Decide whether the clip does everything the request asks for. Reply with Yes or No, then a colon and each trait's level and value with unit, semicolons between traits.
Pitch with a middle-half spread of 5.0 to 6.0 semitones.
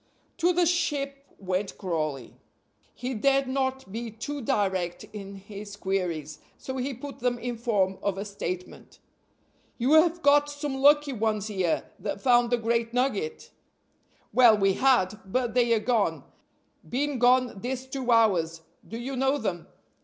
Yes: average, 5.3 semitones